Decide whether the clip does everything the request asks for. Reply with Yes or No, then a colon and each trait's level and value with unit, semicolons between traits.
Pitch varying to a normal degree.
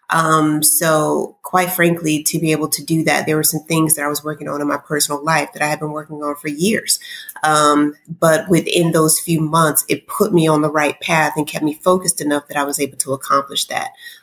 No: narrow, 1.9 semitones